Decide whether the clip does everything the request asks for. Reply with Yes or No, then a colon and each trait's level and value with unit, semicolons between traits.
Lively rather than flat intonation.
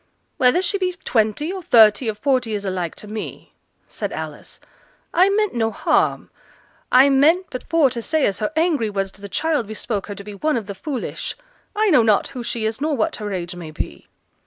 Yes: wide, 6.9 semitones